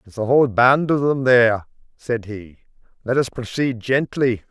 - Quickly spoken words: No, average, 175 wpm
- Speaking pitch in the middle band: No, low, 120 Hz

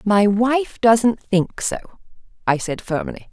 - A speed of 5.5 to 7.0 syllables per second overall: No, 3.6 syllables/s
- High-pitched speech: Yes, high, 215 Hz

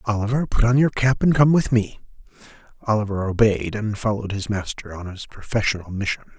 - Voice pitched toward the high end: No, low, 110 Hz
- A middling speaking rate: Yes, average, 180 wpm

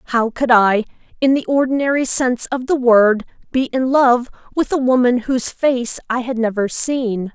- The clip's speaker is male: No, female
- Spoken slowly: No, average, 180 wpm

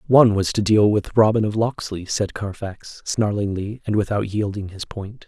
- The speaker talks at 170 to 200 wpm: Yes, average, 180 wpm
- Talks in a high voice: No, low, 105 Hz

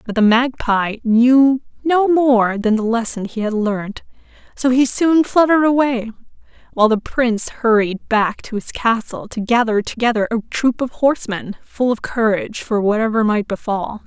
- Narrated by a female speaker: Yes, female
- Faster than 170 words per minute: No, average, 165 wpm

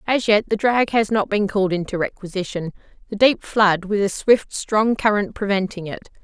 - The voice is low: No, high, 205 Hz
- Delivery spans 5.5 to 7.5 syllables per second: No, 5.1 syllables/s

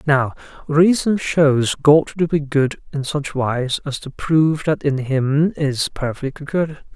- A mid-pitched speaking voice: Yes, medium, 145 Hz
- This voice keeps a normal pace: Yes, average, 165 wpm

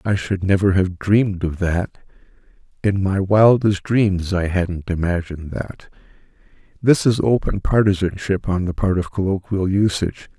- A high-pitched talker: No, very low, 95 Hz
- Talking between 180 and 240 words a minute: No, average, 145 wpm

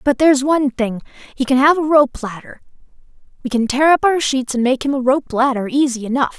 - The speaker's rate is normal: No, fast, 225 wpm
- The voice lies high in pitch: Yes, very high, 265 Hz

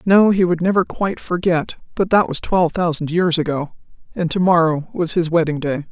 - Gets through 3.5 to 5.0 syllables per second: No, 5.4 syllables/s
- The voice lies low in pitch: No, medium, 170 Hz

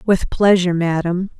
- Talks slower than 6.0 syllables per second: Yes, 5.0 syllables/s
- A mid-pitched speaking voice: Yes, medium, 180 Hz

